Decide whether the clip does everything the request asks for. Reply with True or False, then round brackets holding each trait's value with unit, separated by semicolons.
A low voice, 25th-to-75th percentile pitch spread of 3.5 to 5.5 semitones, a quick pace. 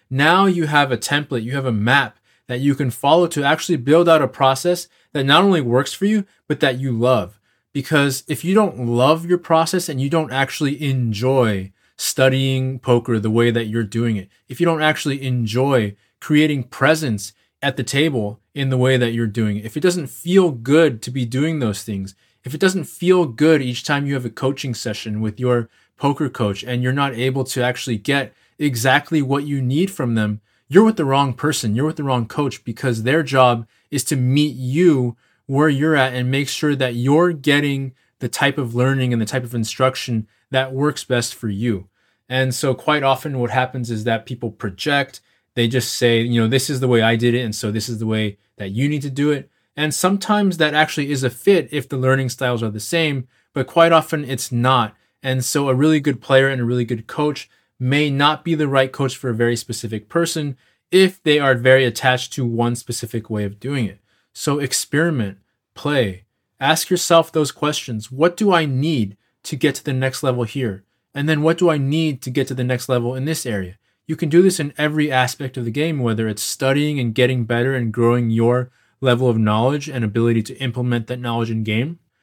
True (130 Hz; 3.8 semitones; 215 wpm)